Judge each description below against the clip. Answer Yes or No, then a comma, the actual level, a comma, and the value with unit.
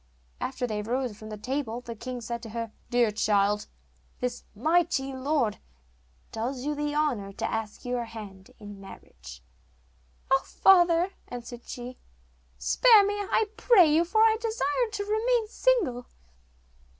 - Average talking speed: Yes, average, 145 wpm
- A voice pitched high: Yes, very high, 255 Hz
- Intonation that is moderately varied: No, wide, 7.8 semitones